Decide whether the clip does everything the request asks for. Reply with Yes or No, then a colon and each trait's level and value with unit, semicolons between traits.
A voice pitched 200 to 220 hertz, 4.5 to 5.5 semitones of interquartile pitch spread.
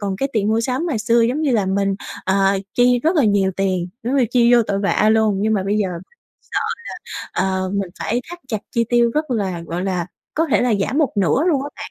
No: high, 215 Hz; average, 4.1 semitones